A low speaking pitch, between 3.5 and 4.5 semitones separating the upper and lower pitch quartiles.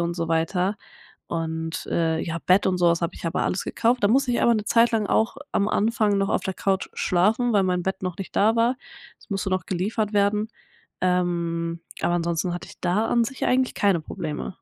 No: high, 190 Hz; average, 3.9 semitones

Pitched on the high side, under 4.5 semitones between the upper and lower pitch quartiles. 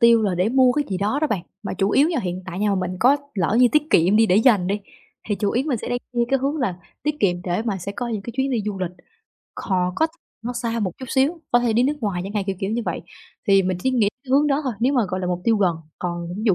No: high, 215 Hz; average, 5.3 semitones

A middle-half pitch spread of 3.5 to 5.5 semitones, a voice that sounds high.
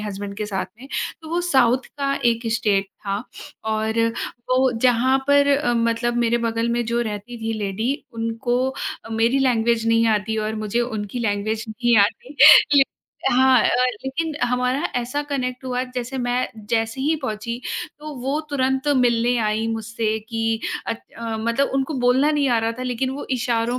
No: narrow, 2.5 semitones; high, 240 Hz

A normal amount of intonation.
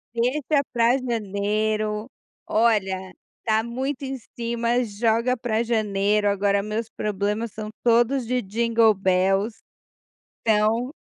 No: narrow, 2.3 semitones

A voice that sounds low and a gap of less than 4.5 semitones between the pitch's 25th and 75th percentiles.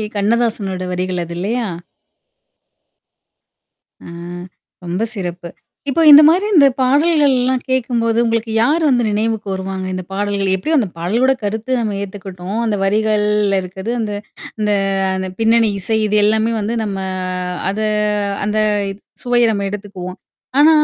No: high, 215 Hz; average, 3.5 semitones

